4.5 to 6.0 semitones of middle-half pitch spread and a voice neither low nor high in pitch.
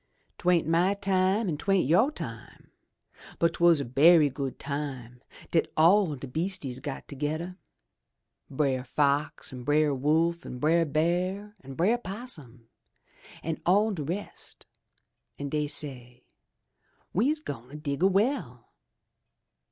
Yes: average, 4.9 semitones; medium, 155 Hz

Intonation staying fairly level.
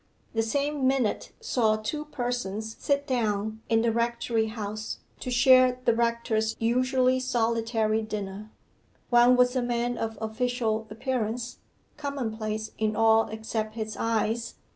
Yes: narrow, 2.2 semitones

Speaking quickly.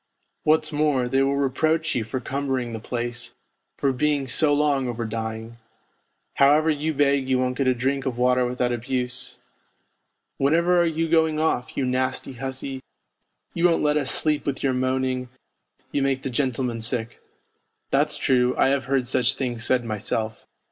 No: average, 175 wpm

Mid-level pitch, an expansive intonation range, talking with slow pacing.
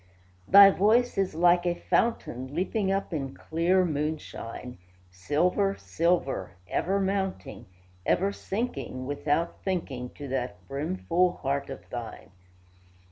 Yes: medium, 170 Hz; wide, 5.9 semitones; slow, 115 wpm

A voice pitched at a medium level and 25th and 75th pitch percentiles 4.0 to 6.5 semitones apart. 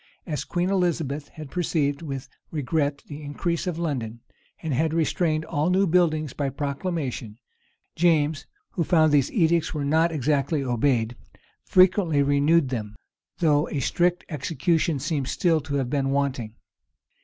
No: medium, 150 Hz; average, 3.1 semitones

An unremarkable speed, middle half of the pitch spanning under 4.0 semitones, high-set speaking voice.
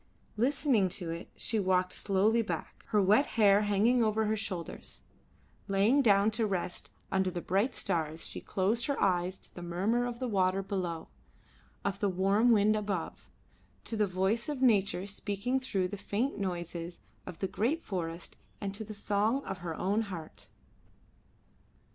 Yes: average, 165 wpm; average, 3.1 semitones; high, 200 Hz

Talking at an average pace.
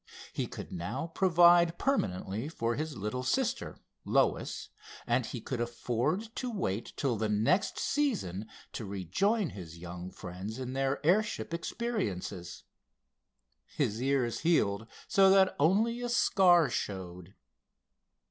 No: slow, 125 wpm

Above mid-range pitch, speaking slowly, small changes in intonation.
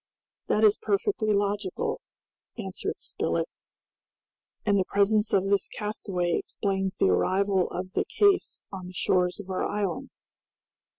Yes: high, 200 Hz; slow, 130 wpm; narrow, 2.0 semitones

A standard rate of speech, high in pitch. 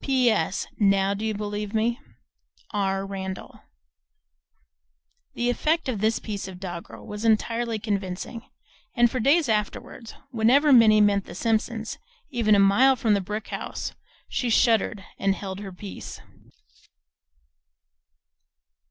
No: slow, 130 wpm; high, 215 Hz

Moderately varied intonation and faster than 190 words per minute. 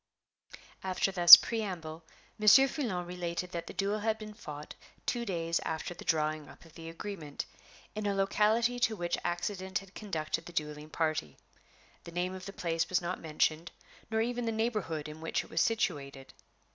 No: average, 4.6 semitones; average, 175 wpm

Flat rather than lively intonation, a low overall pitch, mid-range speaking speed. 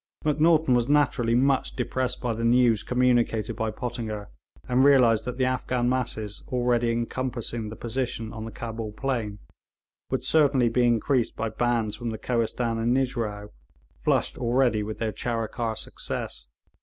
Yes: narrow, 2.2 semitones; low, 120 Hz; average, 150 wpm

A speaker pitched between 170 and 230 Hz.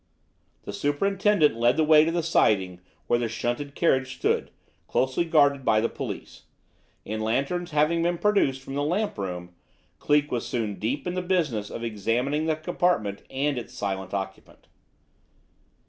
No: low, 135 Hz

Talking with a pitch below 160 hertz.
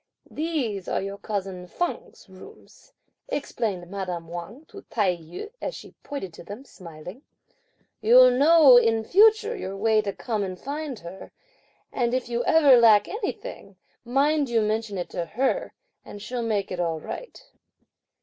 No: high, 225 Hz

